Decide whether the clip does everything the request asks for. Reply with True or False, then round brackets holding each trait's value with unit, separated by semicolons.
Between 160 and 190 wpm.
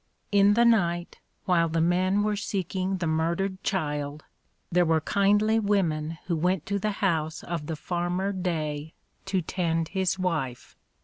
False (150 wpm)